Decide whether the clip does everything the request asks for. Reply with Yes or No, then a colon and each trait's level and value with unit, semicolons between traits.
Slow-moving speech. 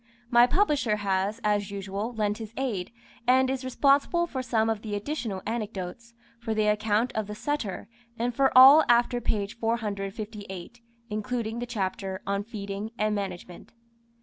No: average, 150 wpm